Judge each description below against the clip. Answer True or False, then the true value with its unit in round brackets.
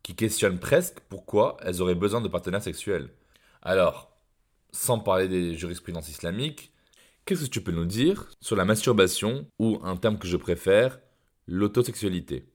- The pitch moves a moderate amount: True (4.1 semitones)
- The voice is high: False (95 Hz)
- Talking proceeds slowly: False (155 wpm)